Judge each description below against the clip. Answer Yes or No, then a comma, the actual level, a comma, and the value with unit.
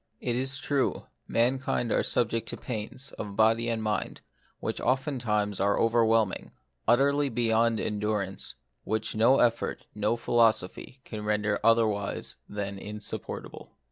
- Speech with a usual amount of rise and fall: No, narrow, 2.3 semitones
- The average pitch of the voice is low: Yes, low, 115 Hz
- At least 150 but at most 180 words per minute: Yes, average, 155 wpm